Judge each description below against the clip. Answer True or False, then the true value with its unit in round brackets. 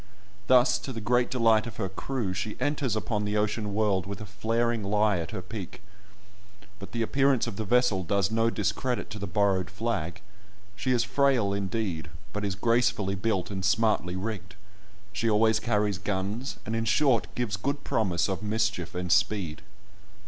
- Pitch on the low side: True (105 Hz)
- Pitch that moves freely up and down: False (3.0 semitones)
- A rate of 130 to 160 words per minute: False (175 wpm)